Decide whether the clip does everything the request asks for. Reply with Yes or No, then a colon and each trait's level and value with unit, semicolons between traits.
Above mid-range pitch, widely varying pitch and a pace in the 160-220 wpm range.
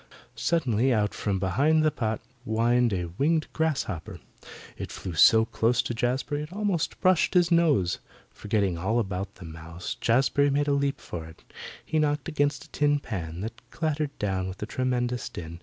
No: low, 120 Hz; wide, 7.2 semitones; average, 175 wpm